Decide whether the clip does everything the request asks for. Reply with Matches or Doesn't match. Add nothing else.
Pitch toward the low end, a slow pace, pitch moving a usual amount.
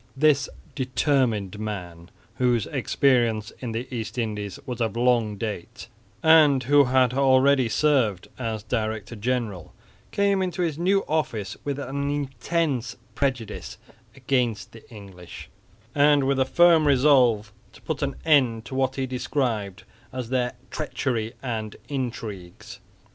Matches